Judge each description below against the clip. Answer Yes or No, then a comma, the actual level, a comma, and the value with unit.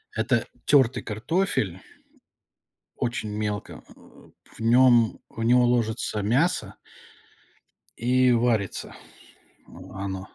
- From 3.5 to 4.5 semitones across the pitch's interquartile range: No, average, 3.0 semitones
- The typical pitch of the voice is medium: No, low, 115 Hz